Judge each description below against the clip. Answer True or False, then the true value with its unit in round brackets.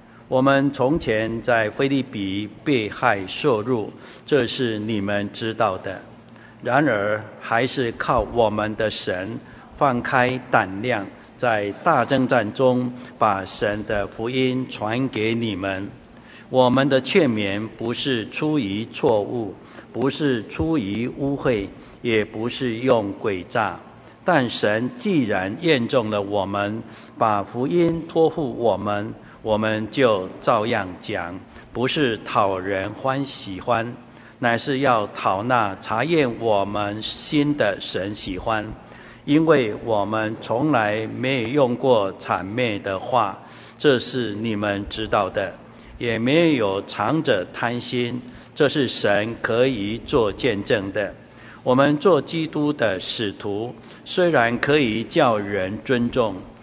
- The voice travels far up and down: False (3.5 semitones)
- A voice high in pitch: False (115 Hz)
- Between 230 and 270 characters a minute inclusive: False (175 characters per minute)